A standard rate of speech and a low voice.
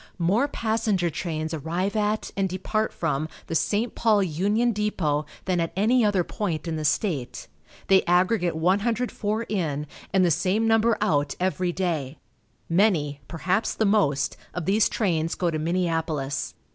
No: average, 150 wpm; medium, 185 Hz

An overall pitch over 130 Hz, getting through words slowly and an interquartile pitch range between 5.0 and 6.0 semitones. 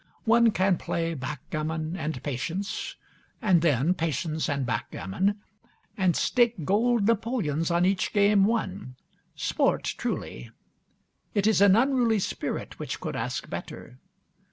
Yes: medium, 185 Hz; slow, 125 wpm; wide, 5.4 semitones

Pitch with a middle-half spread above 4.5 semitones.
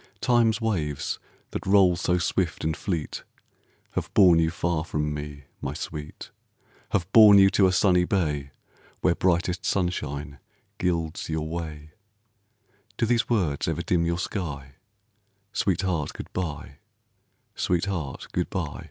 No: average, 3.8 semitones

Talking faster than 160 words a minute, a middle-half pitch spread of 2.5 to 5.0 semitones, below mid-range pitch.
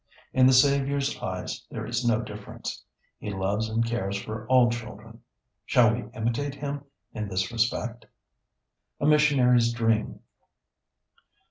No: slow, 135 wpm; average, 2.9 semitones; low, 115 Hz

